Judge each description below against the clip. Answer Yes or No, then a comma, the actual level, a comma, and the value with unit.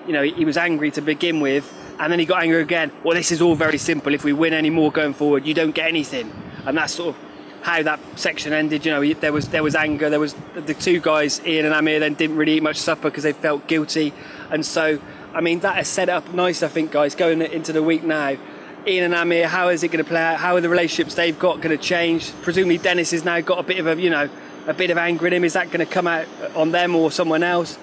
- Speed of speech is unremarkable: No, fast, 265 wpm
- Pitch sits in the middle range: Yes, medium, 160 Hz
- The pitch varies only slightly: Yes, narrow, 1.9 semitones